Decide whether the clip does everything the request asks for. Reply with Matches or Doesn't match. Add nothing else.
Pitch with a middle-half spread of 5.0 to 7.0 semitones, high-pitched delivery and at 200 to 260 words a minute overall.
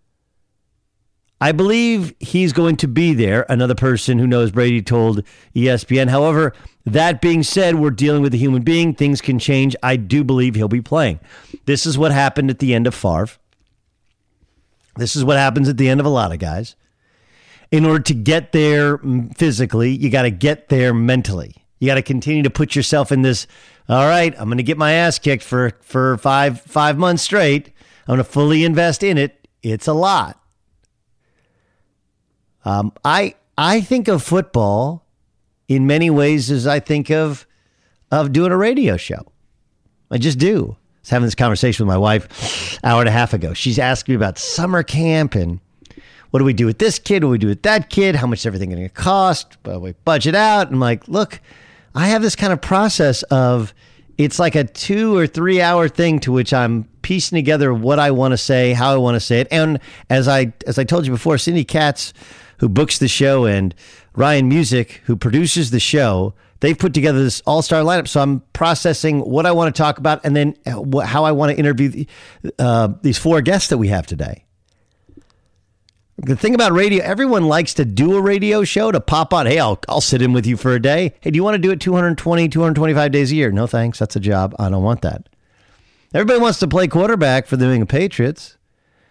Doesn't match